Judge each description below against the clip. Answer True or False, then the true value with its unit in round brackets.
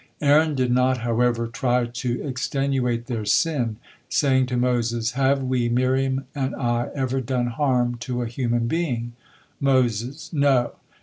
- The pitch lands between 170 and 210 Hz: False (125 Hz)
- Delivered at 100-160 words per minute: True (140 wpm)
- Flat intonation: True (2.1 semitones)